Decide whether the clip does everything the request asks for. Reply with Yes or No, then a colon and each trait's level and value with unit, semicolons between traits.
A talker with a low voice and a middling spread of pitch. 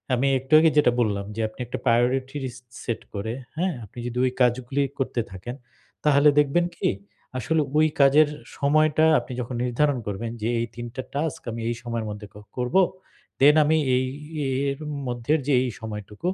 Yes: low, 125 Hz; average, 3.8 semitones